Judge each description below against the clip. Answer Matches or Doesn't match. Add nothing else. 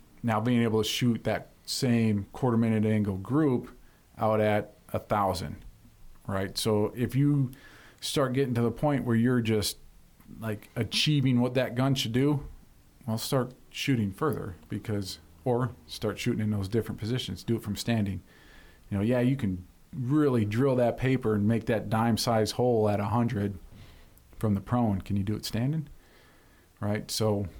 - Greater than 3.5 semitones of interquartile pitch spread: Doesn't match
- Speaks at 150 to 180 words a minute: Matches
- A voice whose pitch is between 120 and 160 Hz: Doesn't match